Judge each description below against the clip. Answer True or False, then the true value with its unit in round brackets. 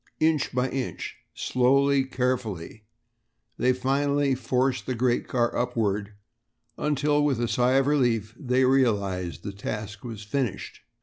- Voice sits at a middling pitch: False (125 Hz)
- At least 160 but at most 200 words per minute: False (135 wpm)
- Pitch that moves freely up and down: False (3.6 semitones)